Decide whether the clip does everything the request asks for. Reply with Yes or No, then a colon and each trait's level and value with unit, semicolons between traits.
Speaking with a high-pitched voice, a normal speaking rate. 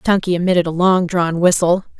No: medium, 175 Hz; average, 180 wpm